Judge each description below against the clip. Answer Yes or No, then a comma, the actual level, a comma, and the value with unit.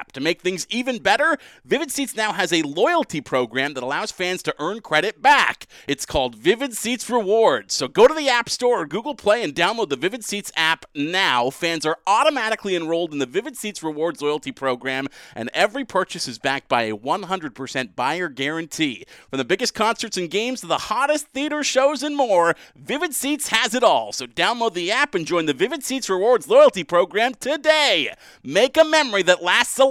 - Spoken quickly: No, average, 195 wpm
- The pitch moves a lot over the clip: Yes, wide, 8.9 semitones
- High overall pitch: Yes, high, 205 Hz